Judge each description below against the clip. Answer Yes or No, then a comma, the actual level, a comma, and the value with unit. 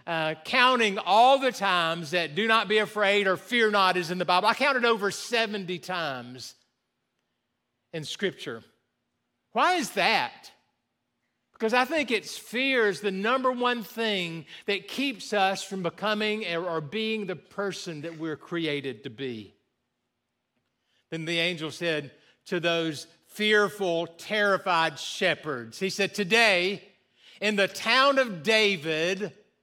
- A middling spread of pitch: Yes, average, 4.6 semitones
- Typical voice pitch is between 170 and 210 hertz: Yes, high, 190 Hz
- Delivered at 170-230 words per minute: No, average, 140 wpm